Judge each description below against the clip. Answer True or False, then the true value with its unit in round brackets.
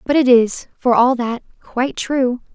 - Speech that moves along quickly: False (190 wpm)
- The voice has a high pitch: True (250 Hz)